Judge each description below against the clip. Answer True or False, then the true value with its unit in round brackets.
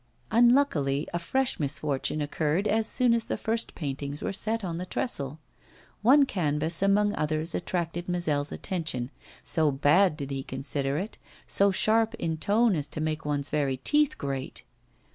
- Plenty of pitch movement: True (6.4 semitones)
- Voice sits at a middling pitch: True (165 Hz)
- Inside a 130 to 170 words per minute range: True (160 wpm)